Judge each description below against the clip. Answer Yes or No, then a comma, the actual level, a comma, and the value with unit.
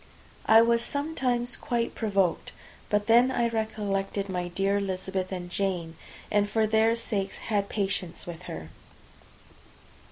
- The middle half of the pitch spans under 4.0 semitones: Yes, average, 3.3 semitones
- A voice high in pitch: Yes, high, 205 Hz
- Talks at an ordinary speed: No, slow, 130 wpm